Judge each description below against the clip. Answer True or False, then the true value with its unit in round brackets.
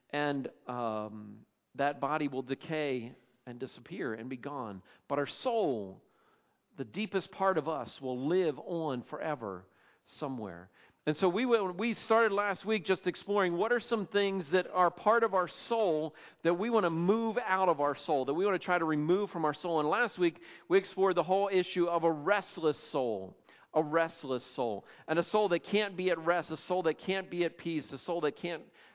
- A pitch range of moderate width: True (4.8 semitones)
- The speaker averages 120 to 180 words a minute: False (200 wpm)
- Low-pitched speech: False (170 Hz)